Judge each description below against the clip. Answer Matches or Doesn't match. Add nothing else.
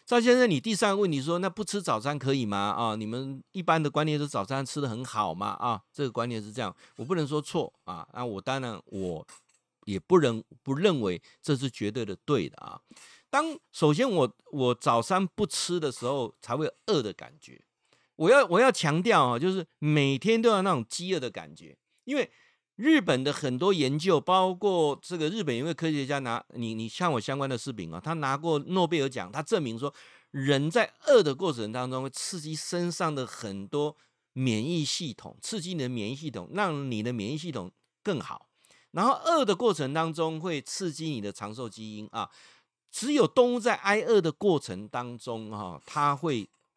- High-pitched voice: Doesn't match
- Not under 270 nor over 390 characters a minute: Matches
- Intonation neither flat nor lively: Doesn't match